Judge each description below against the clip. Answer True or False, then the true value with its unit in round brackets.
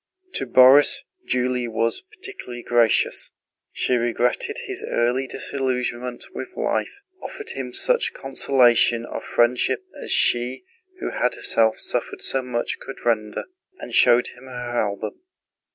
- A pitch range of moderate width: False (2.1 semitones)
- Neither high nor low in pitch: False (125 Hz)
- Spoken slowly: True (130 wpm)